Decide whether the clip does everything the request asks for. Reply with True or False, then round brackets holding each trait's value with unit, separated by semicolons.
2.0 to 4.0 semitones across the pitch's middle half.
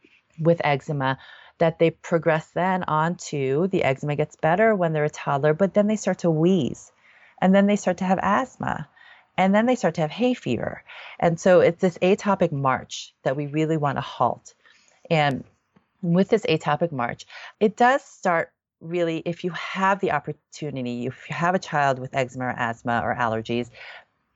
False (4.6 semitones)